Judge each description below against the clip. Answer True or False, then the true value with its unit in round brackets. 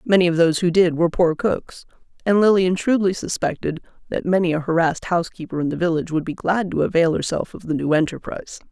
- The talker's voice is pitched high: False (170 Hz)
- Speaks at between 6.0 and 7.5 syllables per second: True (6.4 syllables/s)